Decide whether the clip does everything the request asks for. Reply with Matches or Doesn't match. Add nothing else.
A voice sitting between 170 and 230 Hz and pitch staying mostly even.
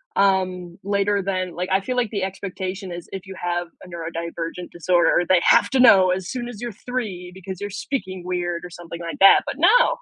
Matches